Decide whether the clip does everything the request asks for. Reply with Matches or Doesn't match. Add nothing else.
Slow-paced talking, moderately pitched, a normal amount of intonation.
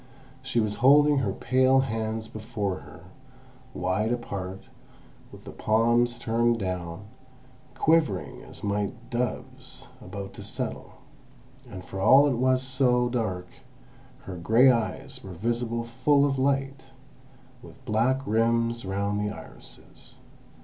Doesn't match